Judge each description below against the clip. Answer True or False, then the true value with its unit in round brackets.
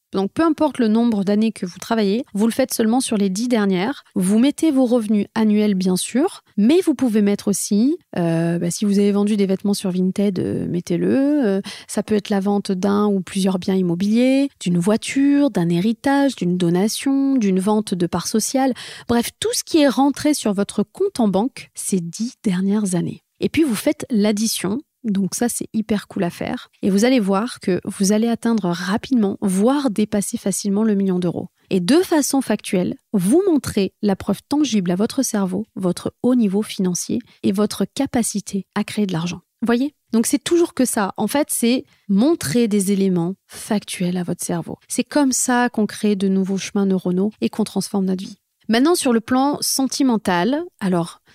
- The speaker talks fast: False (195 wpm)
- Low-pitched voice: False (210 Hz)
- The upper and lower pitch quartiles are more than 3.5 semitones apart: True (4.4 semitones)